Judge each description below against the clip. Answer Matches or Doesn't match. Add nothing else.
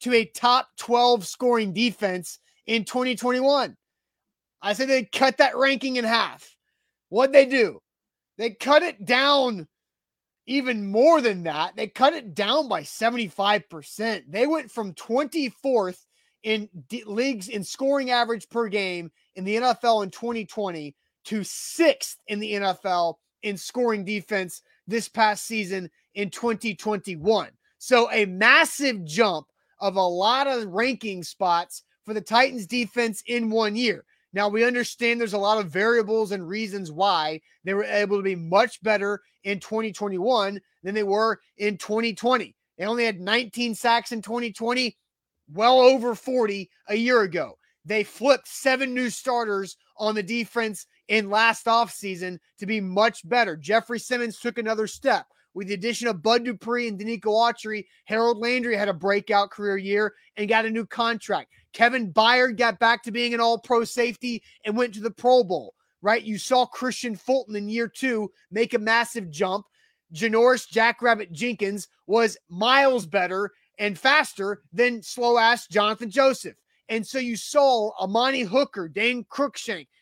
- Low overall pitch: Doesn't match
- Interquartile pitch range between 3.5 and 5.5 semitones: Doesn't match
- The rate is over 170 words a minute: Doesn't match